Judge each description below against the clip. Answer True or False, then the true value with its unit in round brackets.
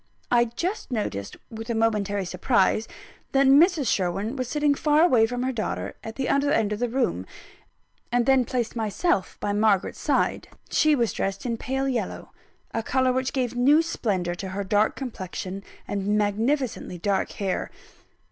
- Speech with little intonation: False (4.6 semitones)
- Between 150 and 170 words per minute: True (165 wpm)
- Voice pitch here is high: True (230 Hz)